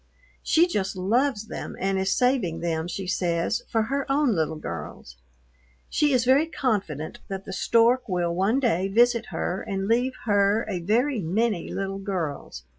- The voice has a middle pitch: No, high, 200 Hz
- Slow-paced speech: No, average, 165 wpm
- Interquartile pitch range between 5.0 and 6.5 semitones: Yes, average, 5.3 semitones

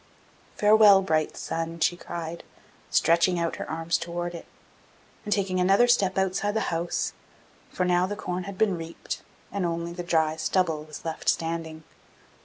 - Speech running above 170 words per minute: No, average, 160 wpm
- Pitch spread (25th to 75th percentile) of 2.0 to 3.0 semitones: Yes, narrow, 2.6 semitones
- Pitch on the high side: No, medium, 175 Hz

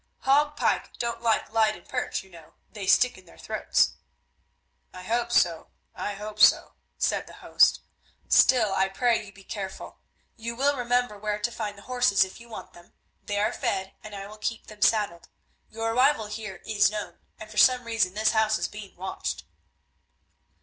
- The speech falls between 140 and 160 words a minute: No, average, 185 wpm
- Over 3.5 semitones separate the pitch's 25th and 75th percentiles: No, average, 2.9 semitones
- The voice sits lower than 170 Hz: No, high, 215 Hz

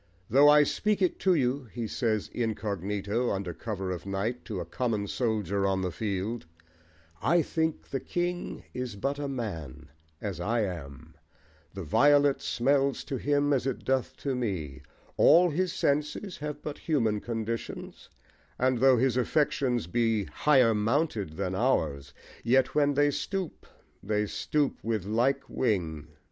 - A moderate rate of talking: Yes, average, 150 wpm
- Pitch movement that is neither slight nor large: No, wide, 5.9 semitones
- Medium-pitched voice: No, low, 120 Hz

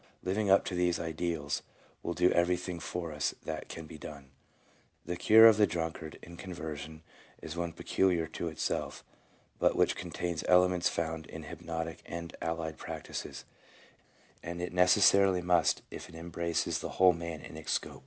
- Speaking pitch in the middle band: No, very low, 85 Hz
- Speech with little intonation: Yes, narrow, 1.8 semitones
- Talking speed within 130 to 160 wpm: No, average, 170 wpm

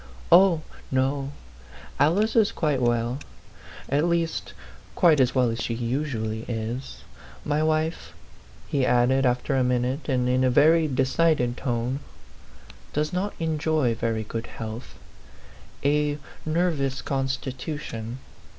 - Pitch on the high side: No, low, 135 Hz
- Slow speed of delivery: Yes, slow, 125 wpm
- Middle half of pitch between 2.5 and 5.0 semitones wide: Yes, average, 4.1 semitones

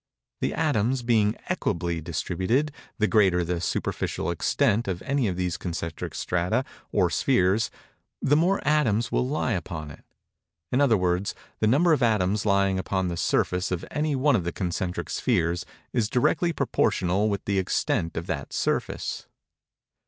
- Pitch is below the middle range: Yes, low, 100 Hz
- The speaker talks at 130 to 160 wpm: Yes, average, 155 wpm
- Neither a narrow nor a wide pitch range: No, wide, 6.0 semitones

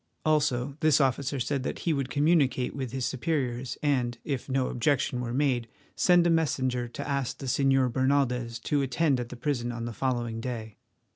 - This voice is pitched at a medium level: No, low, 130 Hz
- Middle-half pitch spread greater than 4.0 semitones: No, average, 2.7 semitones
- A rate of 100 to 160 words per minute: No, average, 185 wpm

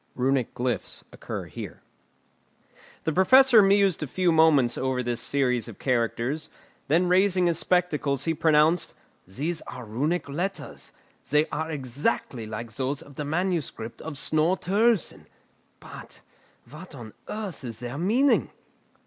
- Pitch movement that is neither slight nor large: No, wide, 5.8 semitones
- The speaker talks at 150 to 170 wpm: No, slow, 135 wpm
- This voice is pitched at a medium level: Yes, medium, 150 Hz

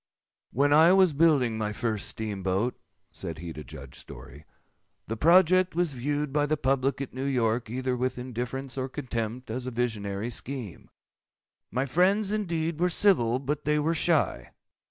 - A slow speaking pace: No, average, 165 wpm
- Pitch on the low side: Yes, low, 130 Hz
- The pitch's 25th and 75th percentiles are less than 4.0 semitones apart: No, average, 5.1 semitones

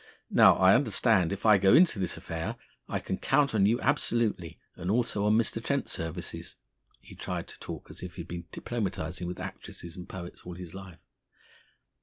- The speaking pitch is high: No, very low, 95 Hz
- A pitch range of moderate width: Yes, average, 4.4 semitones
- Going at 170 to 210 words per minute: Yes, average, 190 wpm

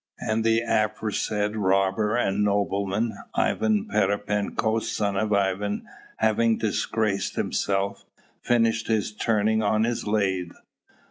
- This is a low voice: Yes, low, 105 Hz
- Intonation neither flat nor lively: No, narrow, 1.7 semitones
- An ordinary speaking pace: No, slow, 110 wpm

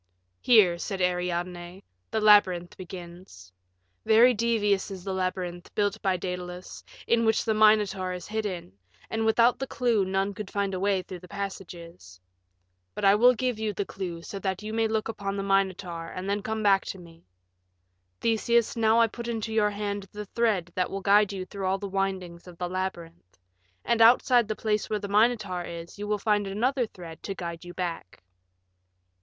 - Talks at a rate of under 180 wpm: No, average, 185 wpm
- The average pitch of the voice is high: Yes, high, 195 Hz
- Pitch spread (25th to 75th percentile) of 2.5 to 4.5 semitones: Yes, average, 3.1 semitones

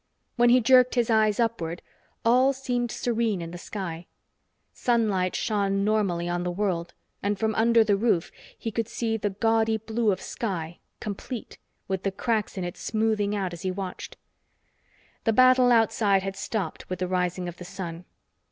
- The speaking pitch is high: Yes, high, 210 Hz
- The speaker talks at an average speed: Yes, average, 170 wpm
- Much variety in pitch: No, average, 3.8 semitones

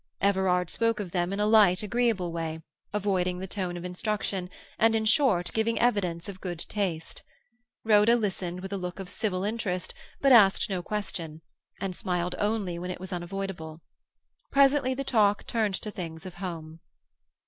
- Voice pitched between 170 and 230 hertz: Yes, high, 190 Hz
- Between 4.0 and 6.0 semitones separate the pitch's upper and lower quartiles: No, average, 3.1 semitones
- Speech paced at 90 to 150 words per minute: No, average, 170 wpm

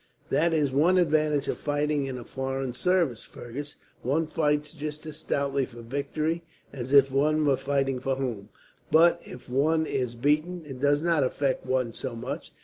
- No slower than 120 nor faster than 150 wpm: No, average, 175 wpm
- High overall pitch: No, medium, 140 Hz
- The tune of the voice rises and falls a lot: No, average, 2.7 semitones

